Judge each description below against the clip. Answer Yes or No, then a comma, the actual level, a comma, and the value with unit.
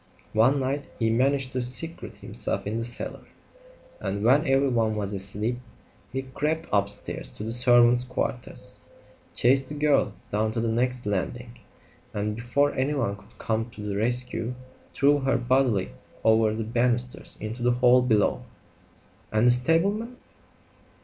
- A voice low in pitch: Yes, low, 120 Hz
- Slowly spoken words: No, average, 145 wpm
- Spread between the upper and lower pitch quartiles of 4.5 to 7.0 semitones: No, average, 3.2 semitones